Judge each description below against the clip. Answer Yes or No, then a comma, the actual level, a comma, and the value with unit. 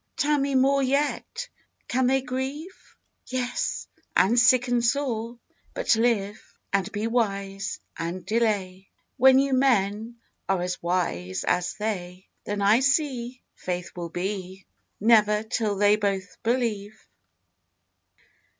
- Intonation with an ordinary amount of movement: Yes, average, 4.7 semitones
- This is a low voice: No, high, 220 Hz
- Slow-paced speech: Yes, slow, 120 wpm